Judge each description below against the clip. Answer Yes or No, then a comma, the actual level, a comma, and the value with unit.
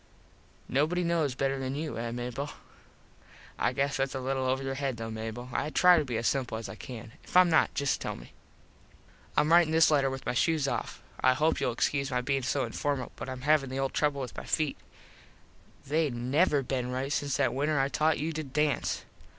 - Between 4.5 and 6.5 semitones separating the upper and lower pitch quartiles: No, average, 2.8 semitones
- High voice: No, low, 135 Hz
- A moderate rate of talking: No, fast, 215 wpm